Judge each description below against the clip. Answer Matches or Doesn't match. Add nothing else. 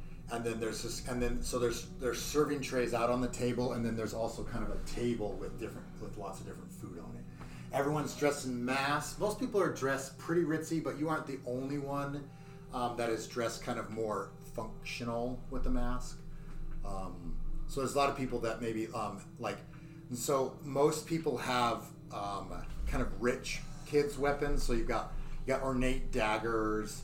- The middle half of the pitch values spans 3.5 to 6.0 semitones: Matches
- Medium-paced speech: Matches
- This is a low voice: Matches